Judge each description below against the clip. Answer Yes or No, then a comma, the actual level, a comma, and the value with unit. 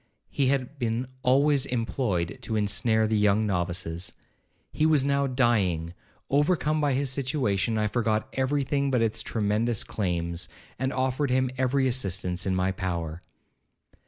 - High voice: No, low, 115 Hz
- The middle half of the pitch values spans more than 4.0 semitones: Yes, wide, 5.6 semitones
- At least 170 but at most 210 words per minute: No, average, 140 wpm